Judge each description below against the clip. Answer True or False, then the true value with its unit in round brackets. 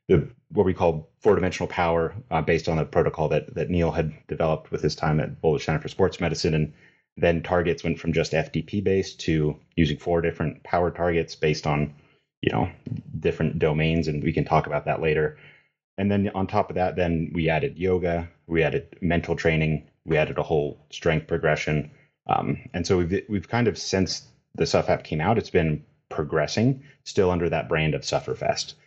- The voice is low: True (85 Hz)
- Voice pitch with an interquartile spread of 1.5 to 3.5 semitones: True (2.5 semitones)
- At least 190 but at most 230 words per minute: True (195 wpm)